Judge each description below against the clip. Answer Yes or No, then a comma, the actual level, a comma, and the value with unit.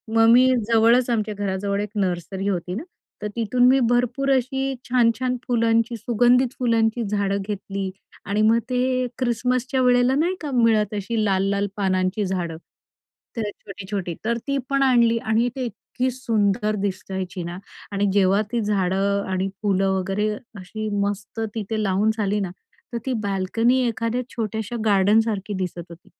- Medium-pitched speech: No, high, 215 Hz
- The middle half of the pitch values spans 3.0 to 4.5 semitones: Yes, average, 3.6 semitones